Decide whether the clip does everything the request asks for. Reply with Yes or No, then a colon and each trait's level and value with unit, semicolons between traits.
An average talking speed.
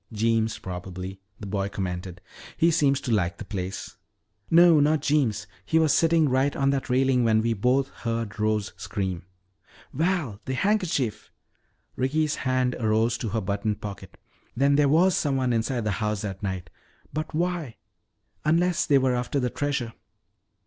Yes: average, 155 wpm